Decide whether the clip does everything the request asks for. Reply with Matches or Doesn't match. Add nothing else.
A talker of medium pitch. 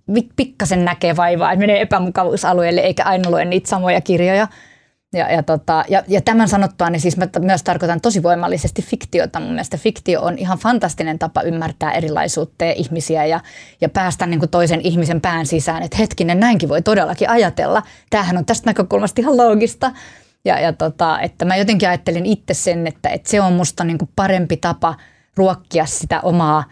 Matches